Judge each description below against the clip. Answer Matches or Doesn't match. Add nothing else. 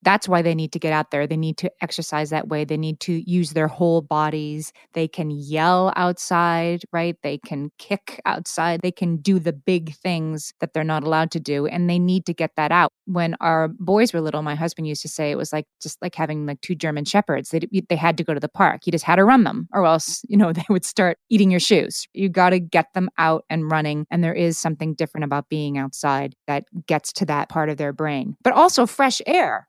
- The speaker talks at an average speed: Doesn't match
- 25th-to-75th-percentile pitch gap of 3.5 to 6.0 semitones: Doesn't match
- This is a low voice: Doesn't match